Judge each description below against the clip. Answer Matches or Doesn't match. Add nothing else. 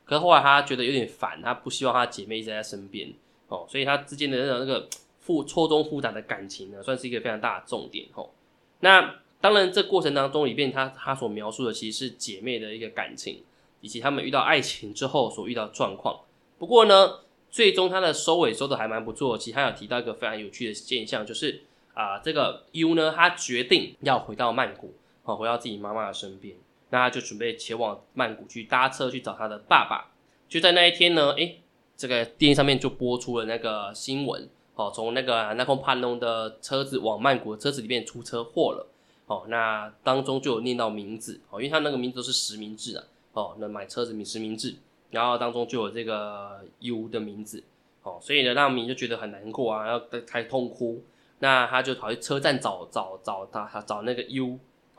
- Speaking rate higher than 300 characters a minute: Matches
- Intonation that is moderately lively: Matches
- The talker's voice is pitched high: Doesn't match